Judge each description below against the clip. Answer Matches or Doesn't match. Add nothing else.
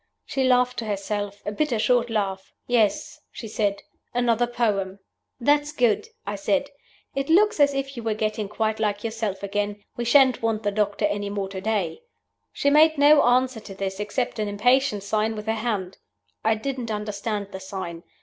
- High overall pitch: Matches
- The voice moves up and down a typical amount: Matches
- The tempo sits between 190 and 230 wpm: Doesn't match